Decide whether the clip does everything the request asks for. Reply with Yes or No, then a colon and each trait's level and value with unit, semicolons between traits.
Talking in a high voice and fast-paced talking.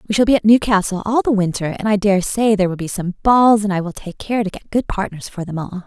Yes: high, 200 Hz; fast, 295 wpm